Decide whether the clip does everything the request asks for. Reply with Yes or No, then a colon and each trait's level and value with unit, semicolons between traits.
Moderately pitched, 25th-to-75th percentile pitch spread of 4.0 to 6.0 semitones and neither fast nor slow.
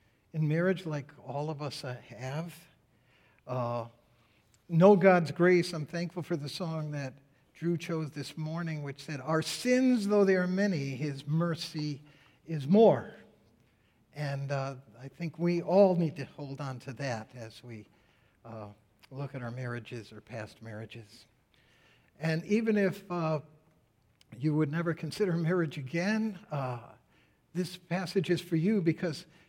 Yes: medium, 150 Hz; average, 5.1 semitones; average, 145 wpm